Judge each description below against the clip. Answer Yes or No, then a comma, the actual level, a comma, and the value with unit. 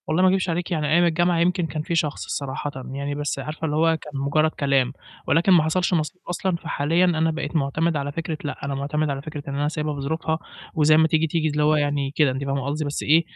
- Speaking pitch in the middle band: Yes, medium, 155 Hz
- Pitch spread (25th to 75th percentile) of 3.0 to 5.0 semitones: No, narrow, 2.5 semitones